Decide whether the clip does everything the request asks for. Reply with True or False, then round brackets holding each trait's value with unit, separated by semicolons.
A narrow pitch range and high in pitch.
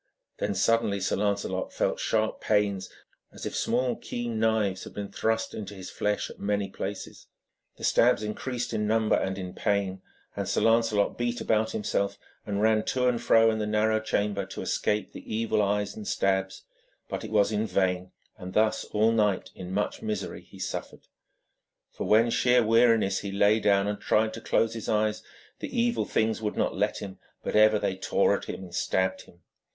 False (2.0 semitones; 105 Hz)